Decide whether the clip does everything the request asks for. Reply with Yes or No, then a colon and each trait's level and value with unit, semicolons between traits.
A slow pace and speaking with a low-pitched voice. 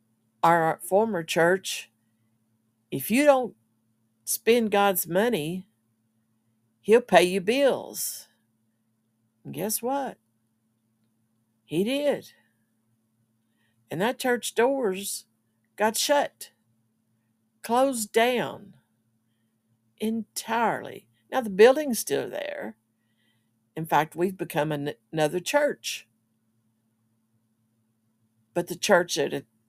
Yes: slow, 90 wpm; low, 115 Hz